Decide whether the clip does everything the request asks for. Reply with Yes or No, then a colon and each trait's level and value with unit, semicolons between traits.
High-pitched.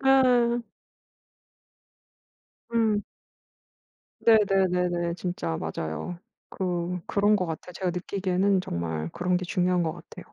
No: medium, 180 Hz